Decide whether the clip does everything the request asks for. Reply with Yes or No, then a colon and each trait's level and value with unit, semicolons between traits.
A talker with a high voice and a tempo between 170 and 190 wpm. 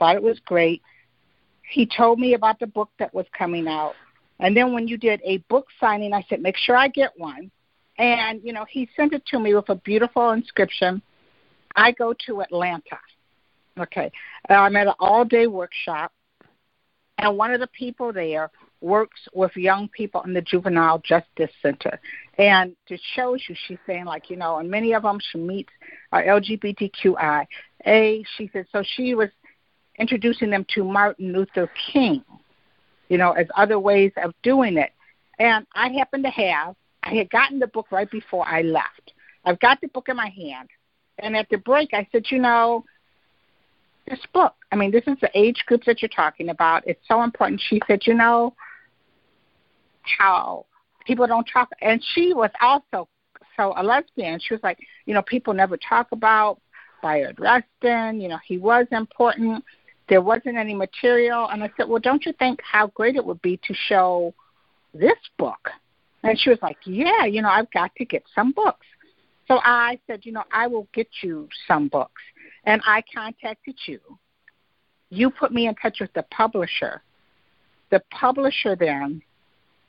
Yes: high, 220 Hz; average, 180 wpm